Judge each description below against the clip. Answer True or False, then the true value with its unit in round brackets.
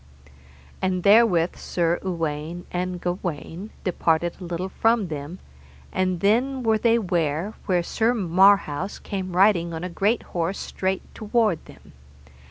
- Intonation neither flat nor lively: True (3.3 semitones)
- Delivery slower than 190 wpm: True (135 wpm)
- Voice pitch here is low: False (185 Hz)